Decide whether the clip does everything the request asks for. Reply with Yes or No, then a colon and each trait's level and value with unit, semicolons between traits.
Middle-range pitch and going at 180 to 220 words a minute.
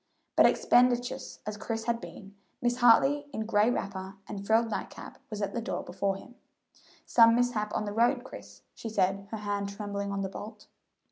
No: high, 215 Hz; average, 190 wpm